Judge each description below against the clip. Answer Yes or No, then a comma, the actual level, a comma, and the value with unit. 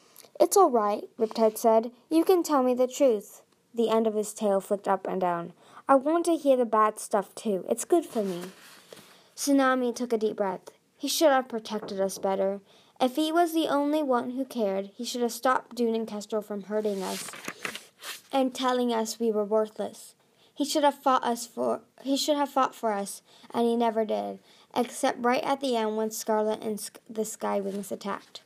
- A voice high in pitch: Yes, high, 230 Hz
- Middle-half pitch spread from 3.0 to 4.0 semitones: Yes, average, 3.7 semitones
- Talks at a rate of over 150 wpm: Yes, average, 200 wpm